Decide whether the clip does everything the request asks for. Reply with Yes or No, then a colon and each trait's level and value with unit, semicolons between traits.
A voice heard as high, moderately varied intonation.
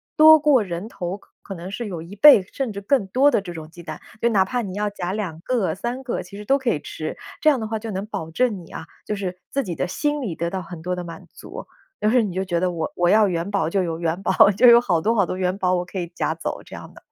Yes: high, 195 Hz; average, 4.6 semitones